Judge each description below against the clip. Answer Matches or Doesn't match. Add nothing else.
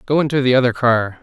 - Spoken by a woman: Doesn't match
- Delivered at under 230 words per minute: Doesn't match